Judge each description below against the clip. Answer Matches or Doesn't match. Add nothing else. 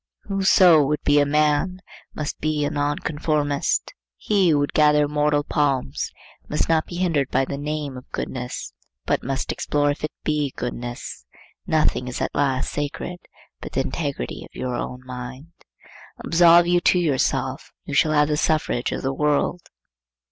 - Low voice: Doesn't match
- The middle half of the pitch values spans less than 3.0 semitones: Matches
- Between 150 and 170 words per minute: Matches